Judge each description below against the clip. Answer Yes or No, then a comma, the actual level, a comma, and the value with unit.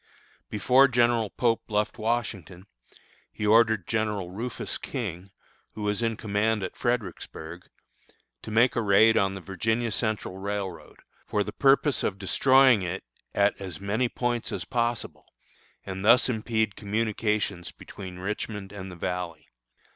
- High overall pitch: No, low, 105 Hz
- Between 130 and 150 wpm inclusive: Yes, average, 140 wpm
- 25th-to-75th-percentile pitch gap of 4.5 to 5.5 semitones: No, average, 3.3 semitones